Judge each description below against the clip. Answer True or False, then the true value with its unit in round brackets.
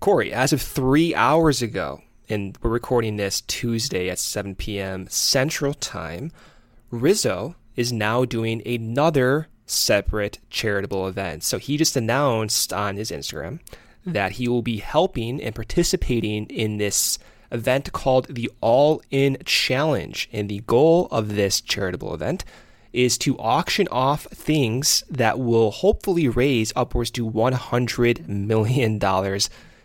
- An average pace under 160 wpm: True (135 wpm)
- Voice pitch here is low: True (115 Hz)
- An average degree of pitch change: True (3.8 semitones)